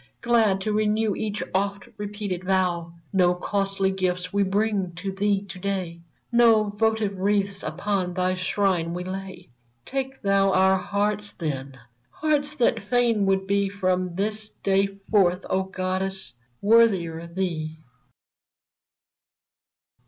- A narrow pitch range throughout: Yes, narrow, 2.1 semitones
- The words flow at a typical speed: No, slow, 130 wpm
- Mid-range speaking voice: No, high, 195 Hz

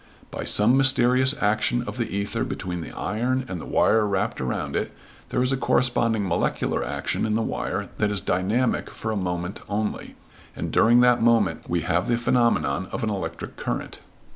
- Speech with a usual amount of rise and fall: Yes, average, 4.3 semitones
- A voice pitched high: No, low, 110 Hz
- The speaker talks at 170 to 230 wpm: Yes, average, 185 wpm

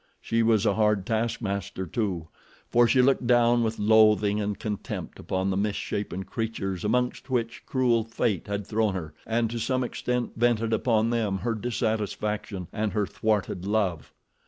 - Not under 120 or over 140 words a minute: No, average, 160 wpm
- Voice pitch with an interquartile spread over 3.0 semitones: No, narrow, 2.5 semitones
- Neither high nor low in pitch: No, low, 110 Hz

